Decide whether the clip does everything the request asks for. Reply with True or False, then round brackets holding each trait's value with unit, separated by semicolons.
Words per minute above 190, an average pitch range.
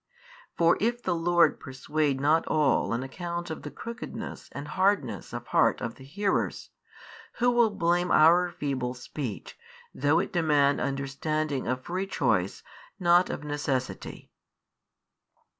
False (135 wpm; 4.3 semitones)